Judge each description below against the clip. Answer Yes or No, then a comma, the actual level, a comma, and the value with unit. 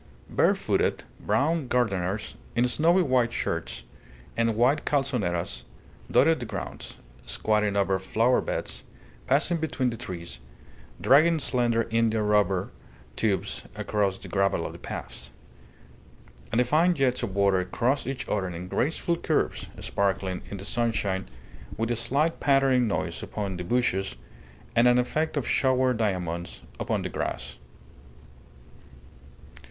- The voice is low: Yes, low, 115 Hz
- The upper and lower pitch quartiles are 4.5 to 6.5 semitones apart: Yes, average, 5.1 semitones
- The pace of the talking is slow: Yes, slow, 130 wpm